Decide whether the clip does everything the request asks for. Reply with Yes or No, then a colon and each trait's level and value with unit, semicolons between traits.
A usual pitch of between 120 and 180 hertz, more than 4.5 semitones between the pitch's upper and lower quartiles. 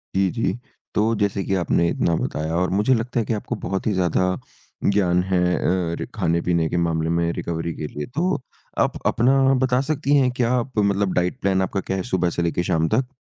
No: very low, 95 Hz; average, 5.0 semitones